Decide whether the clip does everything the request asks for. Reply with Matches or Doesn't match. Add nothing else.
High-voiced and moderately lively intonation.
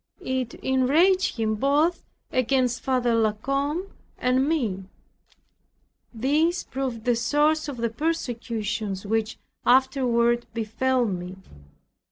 Matches